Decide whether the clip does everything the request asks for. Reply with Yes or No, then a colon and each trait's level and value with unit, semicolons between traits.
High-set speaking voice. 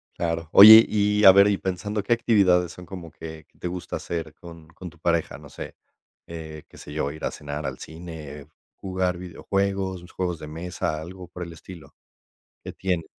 No: very low, 90 Hz